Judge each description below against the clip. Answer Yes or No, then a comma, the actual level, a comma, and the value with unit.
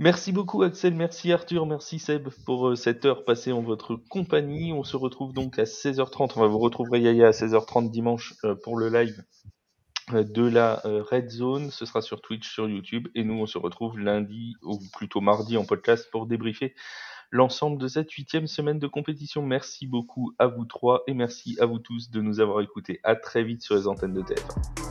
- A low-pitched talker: Yes, low, 120 Hz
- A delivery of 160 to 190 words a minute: No, average, 210 wpm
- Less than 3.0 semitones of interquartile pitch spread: No, average, 3.8 semitones